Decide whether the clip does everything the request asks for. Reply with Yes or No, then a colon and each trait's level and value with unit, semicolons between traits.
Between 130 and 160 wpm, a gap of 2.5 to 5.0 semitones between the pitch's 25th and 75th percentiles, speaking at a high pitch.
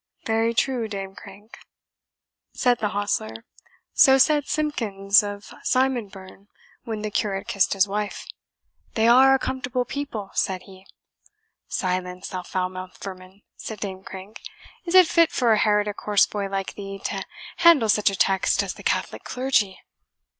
Yes: average, 155 wpm; average, 4.1 semitones; high, 205 Hz